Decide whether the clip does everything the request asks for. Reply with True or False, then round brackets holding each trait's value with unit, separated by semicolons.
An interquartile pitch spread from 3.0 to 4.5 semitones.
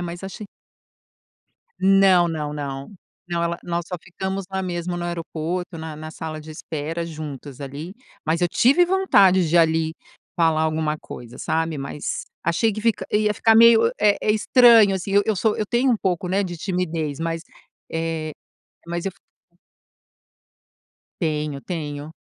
True (3.7 semitones)